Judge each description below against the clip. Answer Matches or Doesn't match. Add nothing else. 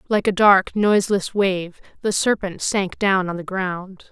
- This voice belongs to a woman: Matches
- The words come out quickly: Doesn't match